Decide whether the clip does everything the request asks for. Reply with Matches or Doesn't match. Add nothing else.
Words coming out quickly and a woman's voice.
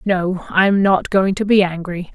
Matches